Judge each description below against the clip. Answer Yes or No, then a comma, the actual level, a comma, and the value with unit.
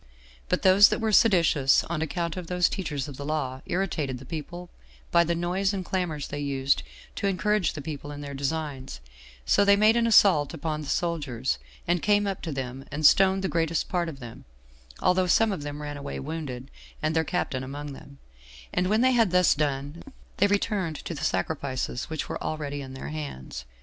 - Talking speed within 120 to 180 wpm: No, average, 200 wpm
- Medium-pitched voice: Yes, medium, 160 Hz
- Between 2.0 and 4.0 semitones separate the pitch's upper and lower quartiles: No, average, 4.5 semitones